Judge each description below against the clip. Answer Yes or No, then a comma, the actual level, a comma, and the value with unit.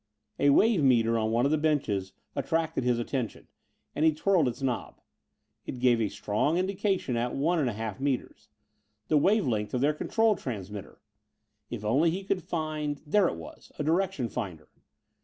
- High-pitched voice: No, medium, 140 Hz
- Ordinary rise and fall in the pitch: No, wide, 5.9 semitones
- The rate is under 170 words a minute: No, average, 175 wpm